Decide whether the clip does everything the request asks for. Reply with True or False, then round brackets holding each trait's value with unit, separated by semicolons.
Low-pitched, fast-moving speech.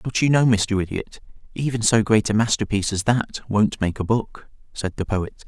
True (105 Hz; 210 wpm)